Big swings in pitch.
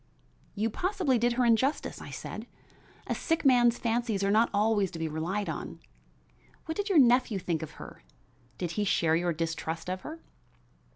Yes: wide, 6.1 semitones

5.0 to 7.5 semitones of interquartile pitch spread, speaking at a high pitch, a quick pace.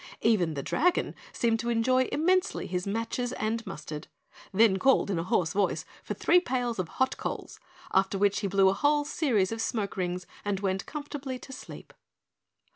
No: average, 5.3 semitones; high, 225 Hz; average, 180 wpm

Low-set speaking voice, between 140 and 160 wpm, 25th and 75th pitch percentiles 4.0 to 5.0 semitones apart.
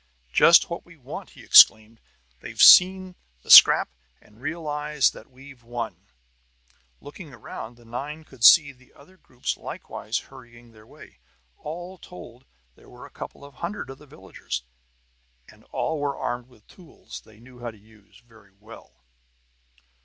Yes: low, 130 Hz; average, 155 wpm; average, 4.6 semitones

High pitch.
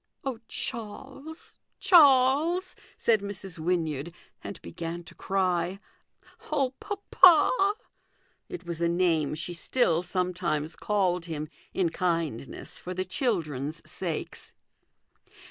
No: medium, 180 Hz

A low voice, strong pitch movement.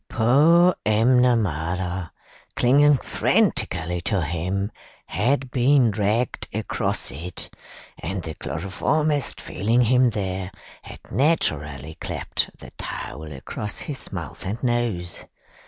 Yes: low, 105 Hz; wide, 6.2 semitones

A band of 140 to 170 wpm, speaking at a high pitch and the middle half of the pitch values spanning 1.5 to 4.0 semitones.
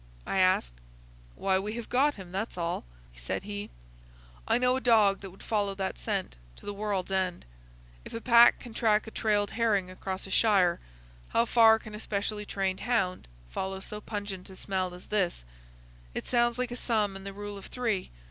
No: average, 195 wpm; high, 205 Hz; average, 2.8 semitones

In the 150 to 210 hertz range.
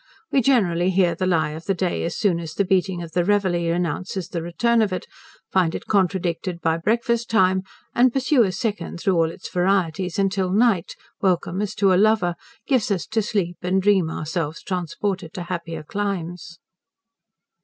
Yes: medium, 185 Hz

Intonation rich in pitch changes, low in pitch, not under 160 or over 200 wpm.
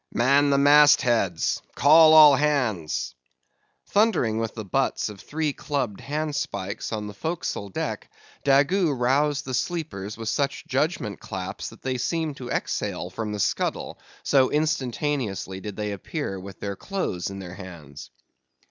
No: wide, 6.6 semitones; low, 130 Hz; average, 150 wpm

